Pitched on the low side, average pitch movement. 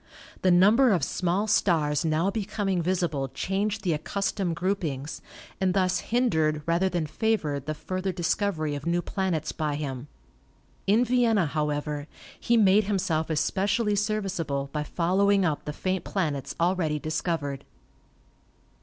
No: medium, 175 Hz; average, 4.5 semitones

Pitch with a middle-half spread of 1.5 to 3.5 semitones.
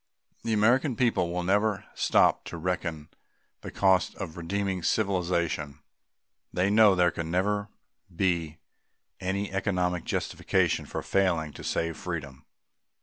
Yes: average, 3.0 semitones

